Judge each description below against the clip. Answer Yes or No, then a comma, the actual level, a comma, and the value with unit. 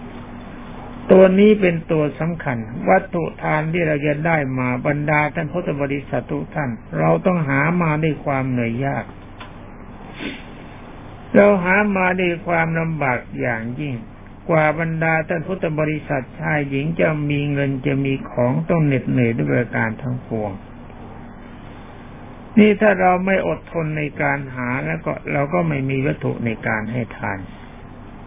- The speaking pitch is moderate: Yes, medium, 145 Hz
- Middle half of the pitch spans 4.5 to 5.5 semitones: Yes, average, 5.1 semitones